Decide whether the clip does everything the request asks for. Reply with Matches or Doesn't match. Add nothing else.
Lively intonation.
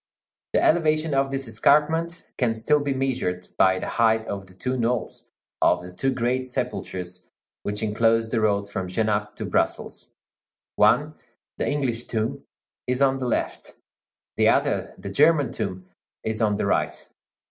Doesn't match